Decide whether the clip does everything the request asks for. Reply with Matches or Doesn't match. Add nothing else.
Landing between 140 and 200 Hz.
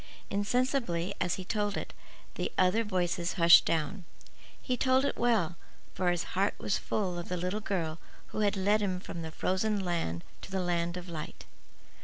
Matches